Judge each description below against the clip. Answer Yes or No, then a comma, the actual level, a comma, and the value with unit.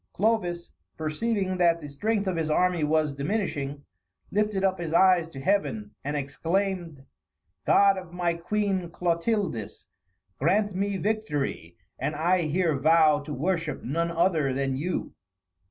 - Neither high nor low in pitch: Yes, medium, 170 Hz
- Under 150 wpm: Yes, average, 140 wpm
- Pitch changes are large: No, average, 4.2 semitones